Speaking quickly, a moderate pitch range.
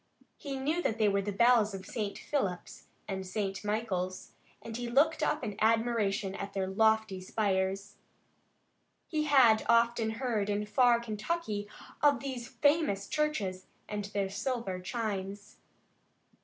No: average, 140 wpm; average, 3.6 semitones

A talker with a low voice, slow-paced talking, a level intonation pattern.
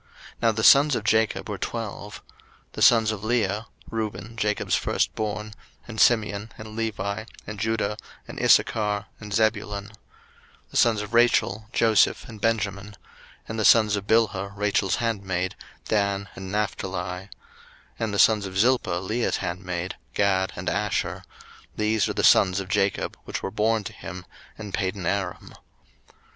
No: low, 105 Hz; average, 155 wpm; narrow, 2.1 semitones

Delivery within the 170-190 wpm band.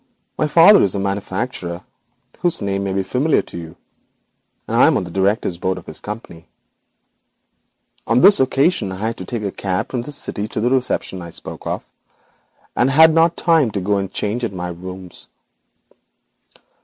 Yes: average, 175 wpm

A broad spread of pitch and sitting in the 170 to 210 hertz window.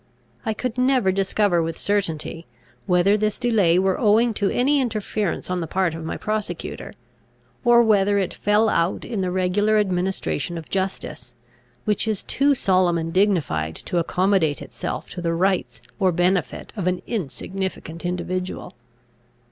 No: average, 3.3 semitones; high, 190 Hz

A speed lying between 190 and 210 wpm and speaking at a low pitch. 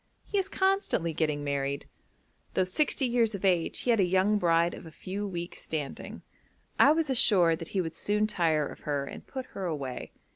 No: average, 195 wpm; medium, 180 Hz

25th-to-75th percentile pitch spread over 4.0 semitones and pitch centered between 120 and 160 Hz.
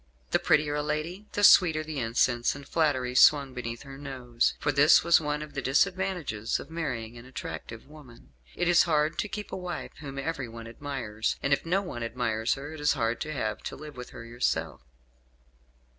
Yes: average, 4.4 semitones; medium, 140 Hz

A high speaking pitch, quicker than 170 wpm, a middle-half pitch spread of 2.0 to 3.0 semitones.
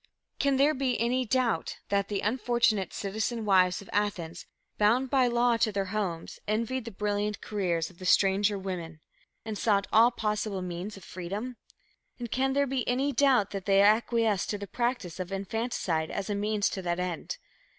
No: high, 210 Hz; average, 180 wpm; average, 3.8 semitones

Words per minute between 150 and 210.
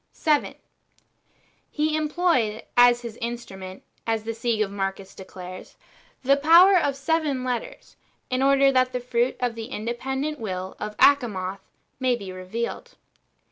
No: average, 140 wpm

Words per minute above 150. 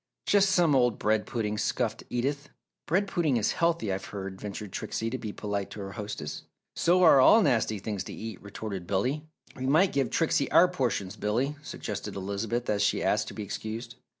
Yes: average, 190 wpm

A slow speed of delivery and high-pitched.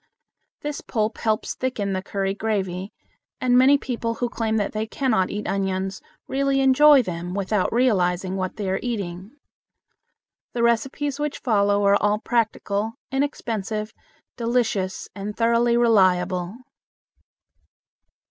Yes: slow, 125 wpm; high, 215 Hz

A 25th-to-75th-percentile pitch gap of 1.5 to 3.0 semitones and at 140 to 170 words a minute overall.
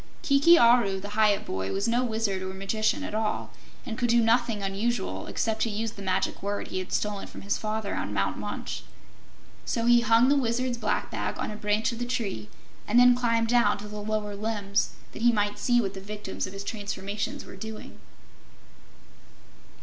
No: average, 2.7 semitones; average, 195 wpm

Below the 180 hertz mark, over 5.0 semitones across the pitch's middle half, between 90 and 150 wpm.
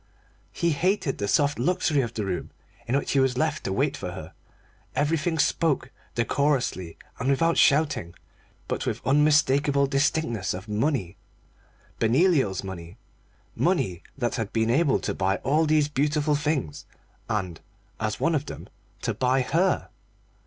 Yes: low, 135 Hz; wide, 5.6 semitones; average, 145 wpm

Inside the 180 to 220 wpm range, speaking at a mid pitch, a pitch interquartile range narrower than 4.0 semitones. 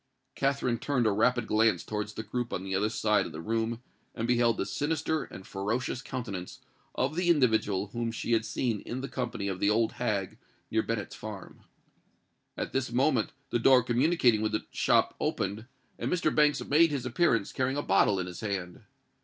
No: average, 190 wpm; low, 115 Hz; average, 3.6 semitones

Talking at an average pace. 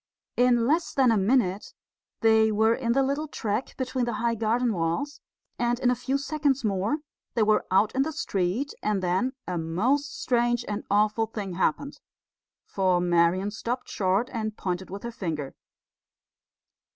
Yes: average, 165 wpm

